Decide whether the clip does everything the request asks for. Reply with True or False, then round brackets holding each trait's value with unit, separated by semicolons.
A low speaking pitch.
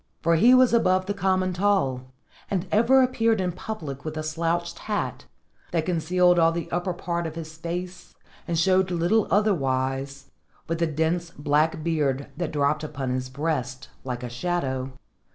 False (165 Hz)